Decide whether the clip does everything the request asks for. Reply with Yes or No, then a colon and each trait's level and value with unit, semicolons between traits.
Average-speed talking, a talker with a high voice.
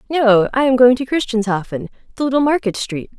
Yes: average, 190 wpm; high, 240 Hz